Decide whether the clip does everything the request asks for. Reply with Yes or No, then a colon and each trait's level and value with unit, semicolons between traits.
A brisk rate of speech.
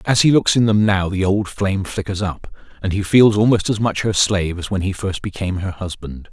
Yes: fast, 245 wpm